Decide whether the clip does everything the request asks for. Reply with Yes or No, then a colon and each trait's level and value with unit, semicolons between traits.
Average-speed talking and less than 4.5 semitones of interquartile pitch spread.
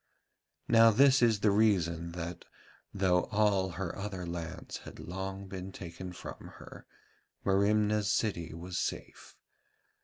No: slow, 125 wpm; average, 3.0 semitones